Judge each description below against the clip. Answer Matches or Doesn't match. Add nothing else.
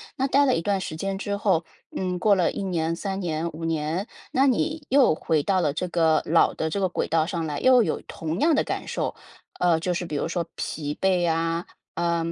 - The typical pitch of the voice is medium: Matches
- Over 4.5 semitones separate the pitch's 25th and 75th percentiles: Doesn't match